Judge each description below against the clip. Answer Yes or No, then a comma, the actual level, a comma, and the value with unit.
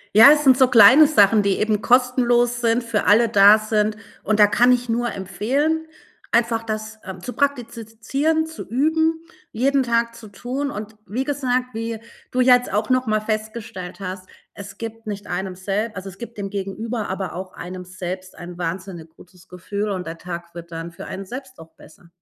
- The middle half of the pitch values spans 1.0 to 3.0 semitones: No, average, 4.4 semitones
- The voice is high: Yes, high, 220 Hz